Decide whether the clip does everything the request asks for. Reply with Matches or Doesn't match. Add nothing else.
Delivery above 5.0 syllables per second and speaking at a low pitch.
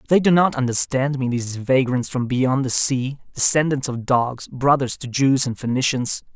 Doesn't match